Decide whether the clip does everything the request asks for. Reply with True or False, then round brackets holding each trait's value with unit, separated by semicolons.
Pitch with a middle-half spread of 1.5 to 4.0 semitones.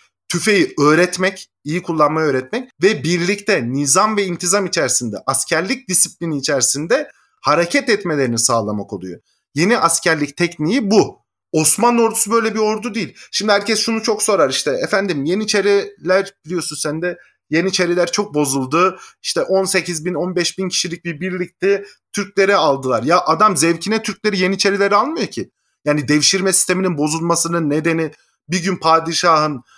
False (4.4 semitones)